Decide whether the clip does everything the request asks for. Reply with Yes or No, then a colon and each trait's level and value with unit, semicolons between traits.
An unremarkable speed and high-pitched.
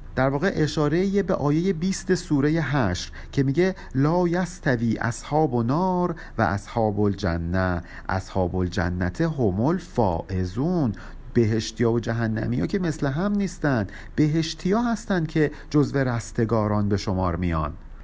No: average, 125 wpm; low, 125 Hz